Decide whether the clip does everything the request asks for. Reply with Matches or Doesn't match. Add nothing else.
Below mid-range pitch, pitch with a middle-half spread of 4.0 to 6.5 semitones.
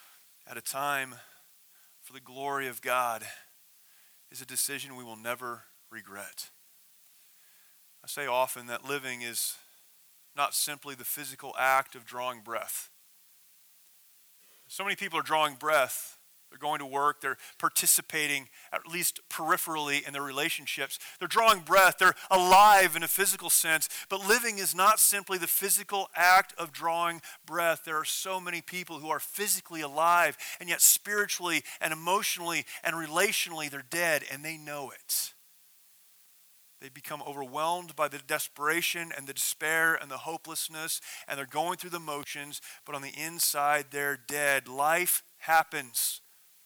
Doesn't match